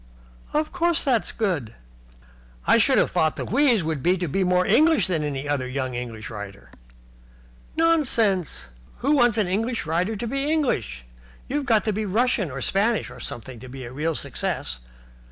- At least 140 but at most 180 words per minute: Yes, average, 175 wpm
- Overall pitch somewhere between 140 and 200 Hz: Yes, high, 190 Hz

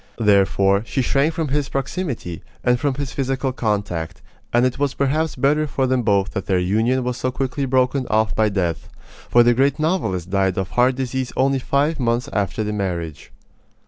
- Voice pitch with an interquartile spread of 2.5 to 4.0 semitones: No, average, 5.3 semitones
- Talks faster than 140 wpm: Yes, average, 185 wpm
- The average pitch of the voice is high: No, low, 125 Hz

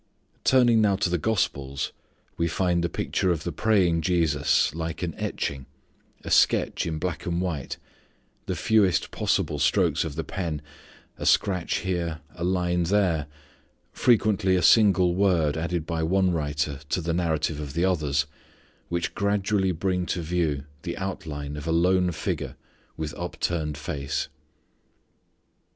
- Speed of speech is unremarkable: Yes, average, 145 wpm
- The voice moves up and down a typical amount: Yes, average, 3.1 semitones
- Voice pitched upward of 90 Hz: No, very low, 85 Hz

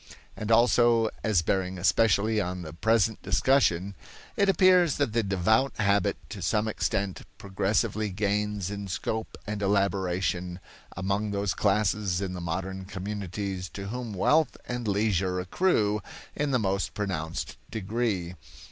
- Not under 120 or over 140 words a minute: Yes, slow, 135 wpm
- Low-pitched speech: Yes, low, 100 Hz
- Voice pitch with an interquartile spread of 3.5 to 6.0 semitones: No, average, 2.8 semitones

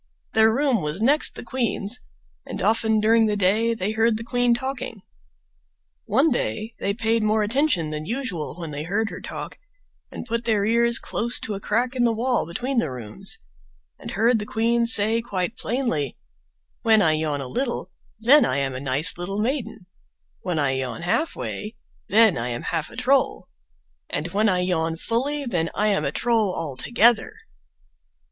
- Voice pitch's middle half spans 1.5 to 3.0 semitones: No, average, 5.1 semitones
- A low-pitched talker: No, high, 220 Hz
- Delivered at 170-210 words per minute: Yes, average, 175 wpm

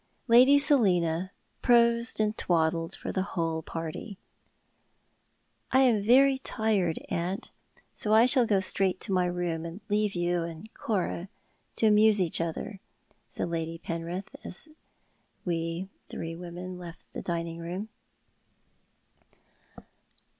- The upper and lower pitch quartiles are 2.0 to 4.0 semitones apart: No, average, 4.4 semitones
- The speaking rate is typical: No, slow, 125 wpm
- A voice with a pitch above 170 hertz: Yes, medium, 185 Hz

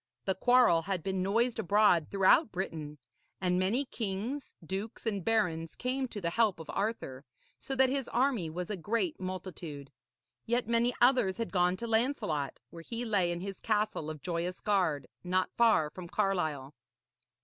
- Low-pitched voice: No, high, 195 Hz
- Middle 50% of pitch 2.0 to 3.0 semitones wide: No, average, 5.2 semitones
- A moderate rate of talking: Yes, average, 165 wpm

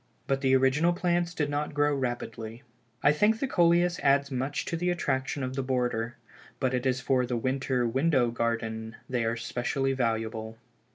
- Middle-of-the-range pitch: No, low, 130 Hz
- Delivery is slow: No, average, 175 wpm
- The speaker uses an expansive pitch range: No, average, 3.3 semitones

